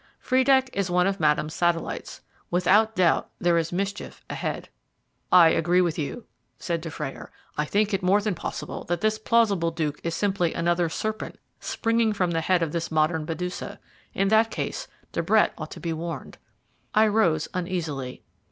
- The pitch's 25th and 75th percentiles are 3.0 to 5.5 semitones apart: Yes, average, 3.8 semitones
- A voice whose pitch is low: No, medium, 175 Hz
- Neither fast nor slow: Yes, average, 170 wpm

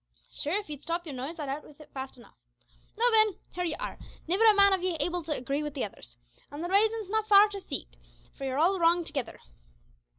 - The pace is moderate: No, fast, 235 wpm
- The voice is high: Yes, very high, 335 Hz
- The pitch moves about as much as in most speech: No, wide, 5.9 semitones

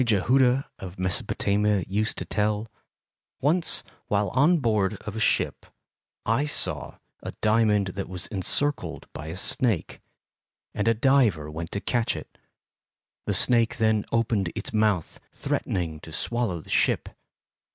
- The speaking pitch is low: Yes, low, 105 Hz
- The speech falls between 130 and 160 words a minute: Yes, average, 140 wpm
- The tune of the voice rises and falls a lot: No, average, 3.9 semitones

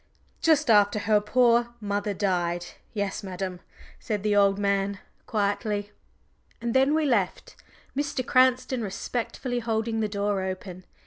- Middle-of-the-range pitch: No, high, 210 Hz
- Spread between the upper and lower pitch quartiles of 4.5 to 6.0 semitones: No, average, 3.1 semitones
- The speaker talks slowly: Yes, slow, 130 wpm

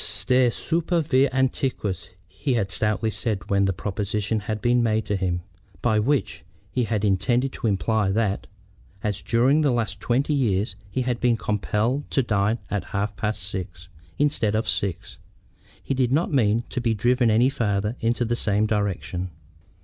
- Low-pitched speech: Yes, low, 110 Hz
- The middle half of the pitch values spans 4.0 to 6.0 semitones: No, average, 3.6 semitones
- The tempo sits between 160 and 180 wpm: Yes, average, 170 wpm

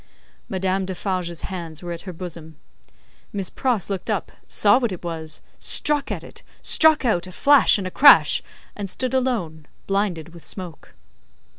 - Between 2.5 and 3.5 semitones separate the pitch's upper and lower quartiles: No, average, 4.1 semitones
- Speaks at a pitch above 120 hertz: Yes, medium, 185 Hz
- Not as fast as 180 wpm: Yes, average, 160 wpm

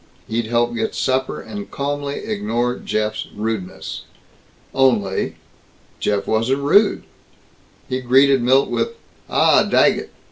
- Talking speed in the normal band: No, slow, 110 wpm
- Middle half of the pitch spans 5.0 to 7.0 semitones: No, average, 3.9 semitones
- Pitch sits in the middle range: No, low, 130 Hz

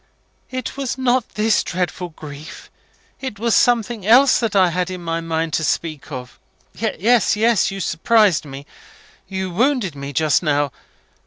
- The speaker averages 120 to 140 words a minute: No, average, 160 wpm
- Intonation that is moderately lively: No, wide, 6.4 semitones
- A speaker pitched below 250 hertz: Yes, medium, 185 Hz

